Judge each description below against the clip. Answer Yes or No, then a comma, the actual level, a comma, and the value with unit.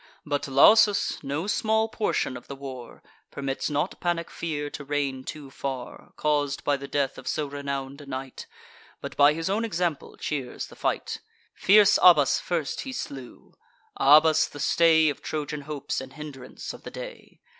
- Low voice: No, medium, 145 Hz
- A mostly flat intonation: No, average, 3.2 semitones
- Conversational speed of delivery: Yes, average, 165 wpm